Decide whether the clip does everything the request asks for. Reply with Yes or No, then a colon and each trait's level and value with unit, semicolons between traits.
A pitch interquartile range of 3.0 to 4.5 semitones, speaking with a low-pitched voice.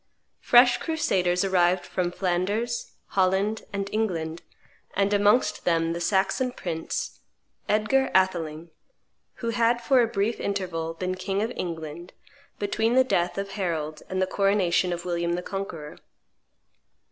No: average, 3.6 semitones; high, 190 Hz